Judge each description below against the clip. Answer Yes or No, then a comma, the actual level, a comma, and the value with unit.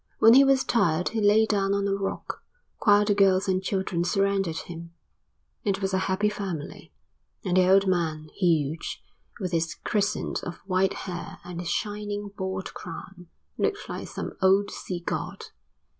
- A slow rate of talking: No, average, 165 wpm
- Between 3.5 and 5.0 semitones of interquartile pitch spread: No, narrow, 2.5 semitones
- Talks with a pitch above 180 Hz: Yes, high, 190 Hz